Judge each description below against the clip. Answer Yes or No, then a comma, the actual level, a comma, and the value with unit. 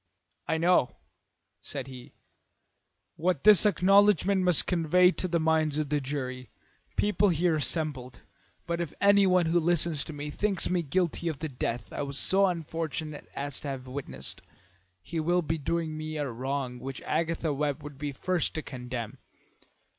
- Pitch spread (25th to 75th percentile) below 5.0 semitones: Yes, average, 4.0 semitones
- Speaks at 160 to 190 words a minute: Yes, average, 170 wpm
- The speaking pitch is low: No, medium, 155 Hz